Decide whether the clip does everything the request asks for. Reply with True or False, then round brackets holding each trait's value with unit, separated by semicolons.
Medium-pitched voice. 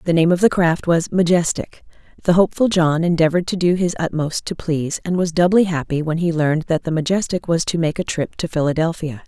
True (170 Hz)